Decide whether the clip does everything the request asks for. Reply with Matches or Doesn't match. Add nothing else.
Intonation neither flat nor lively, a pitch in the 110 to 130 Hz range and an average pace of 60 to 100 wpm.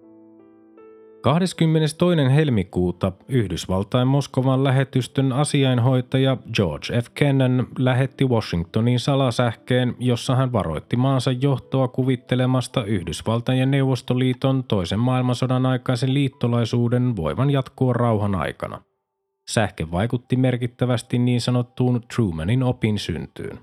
Matches